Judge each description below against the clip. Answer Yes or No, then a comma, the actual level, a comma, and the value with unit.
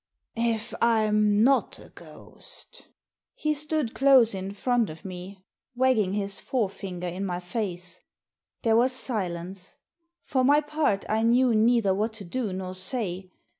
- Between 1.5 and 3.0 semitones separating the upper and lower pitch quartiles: No, average, 4.6 semitones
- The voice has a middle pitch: No, high, 215 Hz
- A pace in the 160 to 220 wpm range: No, average, 150 wpm